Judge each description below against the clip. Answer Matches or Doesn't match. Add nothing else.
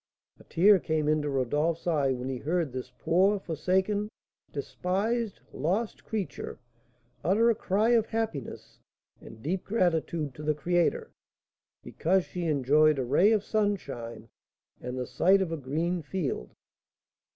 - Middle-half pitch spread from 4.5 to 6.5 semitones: Matches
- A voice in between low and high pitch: Matches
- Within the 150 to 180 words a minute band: Doesn't match